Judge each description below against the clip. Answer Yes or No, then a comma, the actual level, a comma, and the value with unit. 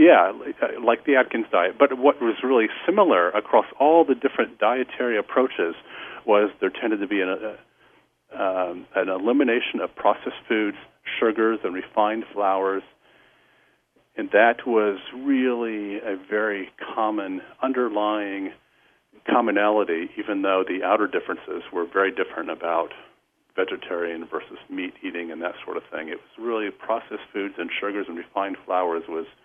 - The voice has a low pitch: Yes, low, 110 Hz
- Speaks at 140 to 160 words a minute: Yes, average, 145 wpm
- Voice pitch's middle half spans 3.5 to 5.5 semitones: Yes, average, 4.9 semitones